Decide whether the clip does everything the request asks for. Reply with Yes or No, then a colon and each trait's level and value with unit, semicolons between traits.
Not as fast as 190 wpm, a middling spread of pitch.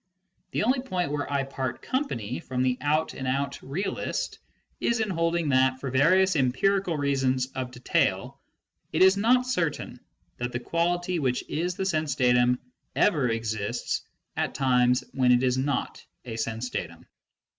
No: average, 155 wpm; wide, 5.8 semitones